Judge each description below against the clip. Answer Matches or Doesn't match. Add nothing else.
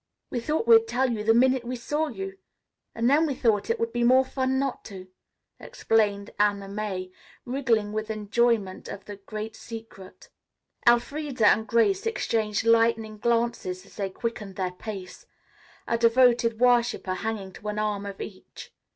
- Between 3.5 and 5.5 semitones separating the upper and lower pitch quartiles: Doesn't match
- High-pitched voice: Matches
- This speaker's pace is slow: Doesn't match